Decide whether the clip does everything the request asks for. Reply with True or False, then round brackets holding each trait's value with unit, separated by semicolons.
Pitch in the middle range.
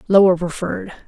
True (155 Hz)